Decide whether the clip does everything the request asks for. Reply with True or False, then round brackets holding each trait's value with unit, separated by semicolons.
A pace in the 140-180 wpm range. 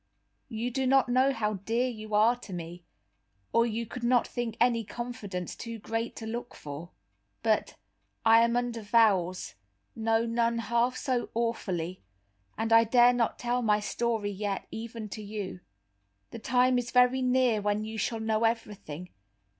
True (160 wpm)